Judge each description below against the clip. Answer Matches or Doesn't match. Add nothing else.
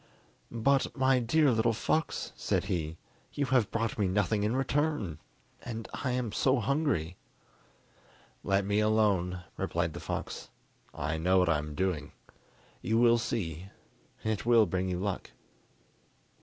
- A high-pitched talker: Doesn't match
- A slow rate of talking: Doesn't match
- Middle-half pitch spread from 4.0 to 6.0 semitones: Matches